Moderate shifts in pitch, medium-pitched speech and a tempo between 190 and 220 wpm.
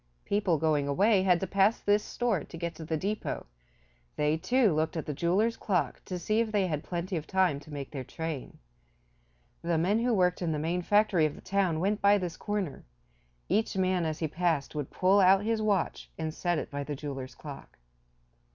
Yes: average, 4.3 semitones; medium, 175 Hz; fast, 205 wpm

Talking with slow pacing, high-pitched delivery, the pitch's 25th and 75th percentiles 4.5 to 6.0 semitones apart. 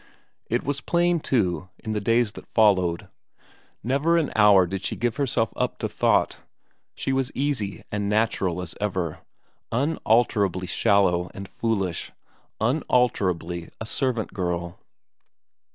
No: slow, 130 wpm; low, 105 Hz; average, 5.1 semitones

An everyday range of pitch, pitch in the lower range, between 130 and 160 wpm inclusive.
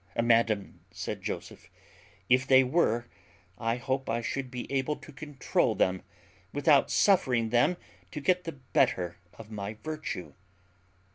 Yes: average, 4.1 semitones; low, 130 Hz; slow, 135 wpm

